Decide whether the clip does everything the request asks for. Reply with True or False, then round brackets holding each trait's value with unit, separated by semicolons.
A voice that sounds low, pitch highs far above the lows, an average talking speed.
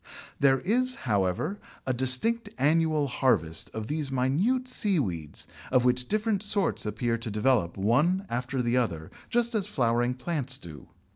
True (130 Hz; 8.1 semitones; 145 wpm)